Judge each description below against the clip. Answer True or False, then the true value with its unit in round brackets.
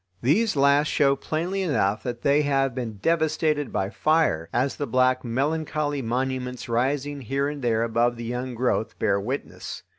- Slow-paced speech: False (160 wpm)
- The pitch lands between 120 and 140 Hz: True (135 Hz)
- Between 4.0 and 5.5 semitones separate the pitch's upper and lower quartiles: False (3.6 semitones)